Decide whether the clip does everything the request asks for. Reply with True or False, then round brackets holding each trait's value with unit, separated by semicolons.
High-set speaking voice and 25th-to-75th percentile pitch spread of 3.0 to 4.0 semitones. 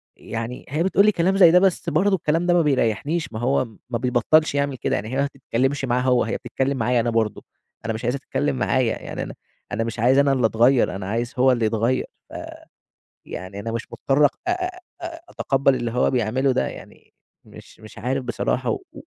False (130 Hz; 3.6 semitones)